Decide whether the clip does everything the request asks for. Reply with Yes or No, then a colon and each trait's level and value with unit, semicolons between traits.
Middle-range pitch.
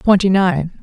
Yes: medium, 180 Hz